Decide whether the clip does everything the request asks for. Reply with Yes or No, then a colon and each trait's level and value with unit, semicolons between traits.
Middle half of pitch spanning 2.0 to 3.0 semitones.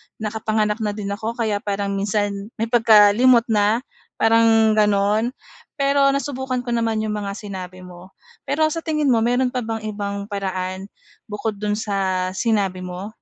Yes: narrow, 2.4 semitones